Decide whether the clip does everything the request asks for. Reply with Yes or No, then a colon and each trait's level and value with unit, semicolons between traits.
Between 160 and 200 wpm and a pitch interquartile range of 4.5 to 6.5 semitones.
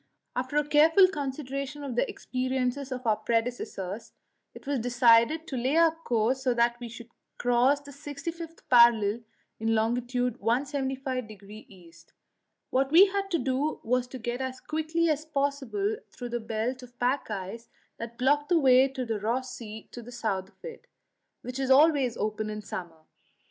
No: average, 165 wpm; average, 3.5 semitones